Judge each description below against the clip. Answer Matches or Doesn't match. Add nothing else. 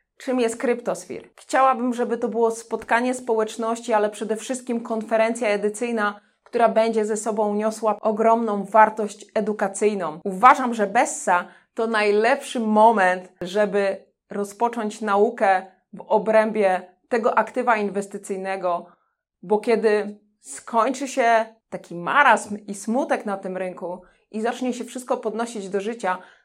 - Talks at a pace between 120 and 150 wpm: Matches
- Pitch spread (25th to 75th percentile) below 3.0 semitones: Matches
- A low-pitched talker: Doesn't match